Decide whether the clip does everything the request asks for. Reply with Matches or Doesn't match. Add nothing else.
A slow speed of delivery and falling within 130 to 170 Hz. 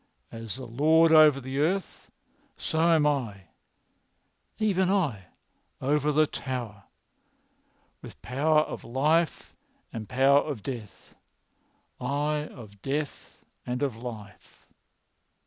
Matches